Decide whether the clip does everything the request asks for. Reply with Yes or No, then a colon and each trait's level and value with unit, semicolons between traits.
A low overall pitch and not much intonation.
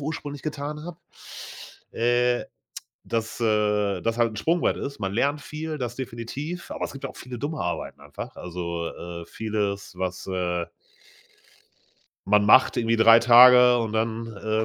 No: low, 115 Hz; average, 4.7 semitones